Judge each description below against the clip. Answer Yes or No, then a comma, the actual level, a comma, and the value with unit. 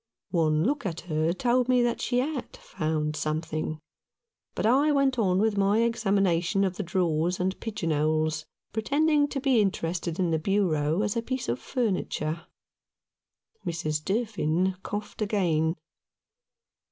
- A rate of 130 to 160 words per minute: Yes, average, 140 wpm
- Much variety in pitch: Yes, wide, 6.3 semitones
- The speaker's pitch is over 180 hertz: Yes, high, 190 Hz